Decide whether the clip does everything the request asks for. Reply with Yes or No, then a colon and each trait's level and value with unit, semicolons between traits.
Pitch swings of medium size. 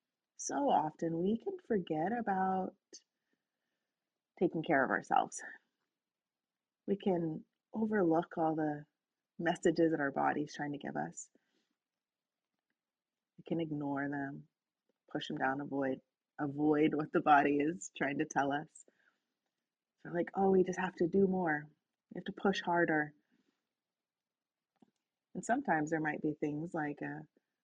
Yes: average, 4.0 semitones